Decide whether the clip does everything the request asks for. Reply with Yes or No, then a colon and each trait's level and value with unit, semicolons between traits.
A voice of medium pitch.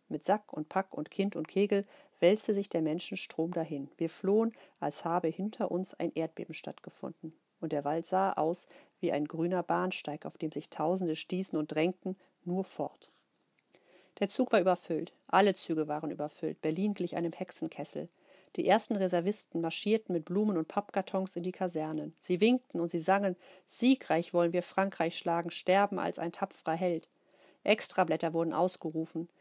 Yes: medium, 180 Hz